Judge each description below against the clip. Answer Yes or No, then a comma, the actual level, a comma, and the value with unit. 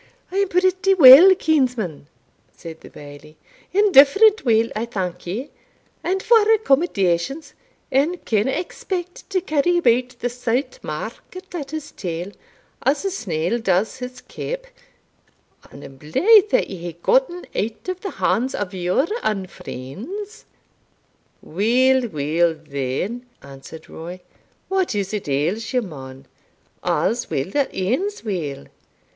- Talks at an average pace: No, slow, 130 wpm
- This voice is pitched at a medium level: No, high, 245 Hz